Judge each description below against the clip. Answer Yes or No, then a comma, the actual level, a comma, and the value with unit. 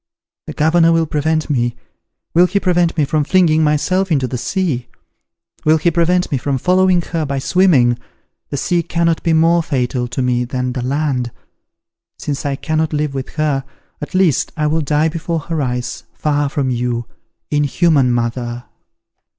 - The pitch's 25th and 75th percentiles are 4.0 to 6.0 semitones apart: Yes, average, 4.3 semitones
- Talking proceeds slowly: No, average, 165 wpm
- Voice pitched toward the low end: No, medium, 150 Hz